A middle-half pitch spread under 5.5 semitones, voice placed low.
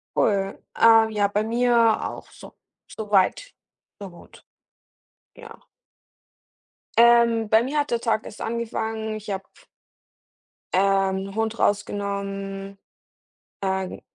No: narrow, 2.5 semitones; high, 215 Hz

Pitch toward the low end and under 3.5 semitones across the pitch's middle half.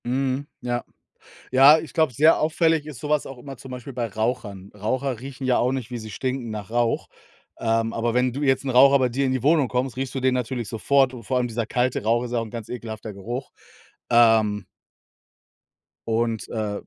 Yes: low, 125 Hz; average, 2.8 semitones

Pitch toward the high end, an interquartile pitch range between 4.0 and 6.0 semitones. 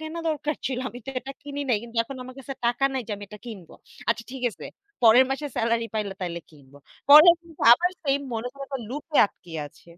Yes: very high, 250 Hz; average, 4.3 semitones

